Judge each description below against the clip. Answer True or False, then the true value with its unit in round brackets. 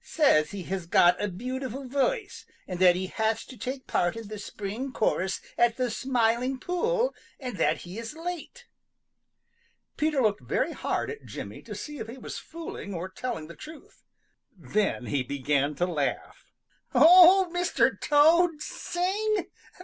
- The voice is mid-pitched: False (250 Hz)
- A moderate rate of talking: True (155 wpm)